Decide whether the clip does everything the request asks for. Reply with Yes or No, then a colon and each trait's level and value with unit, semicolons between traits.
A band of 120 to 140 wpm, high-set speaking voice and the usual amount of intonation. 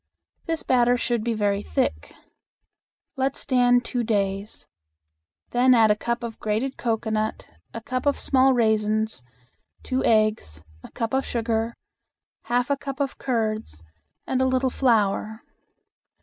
Yes: slow, 135 wpm; high, 235 Hz; average, 3.0 semitones